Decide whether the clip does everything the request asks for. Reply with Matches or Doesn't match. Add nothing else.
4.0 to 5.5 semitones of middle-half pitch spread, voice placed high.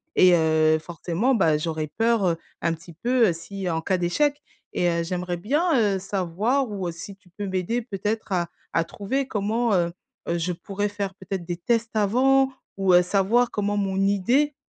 Matches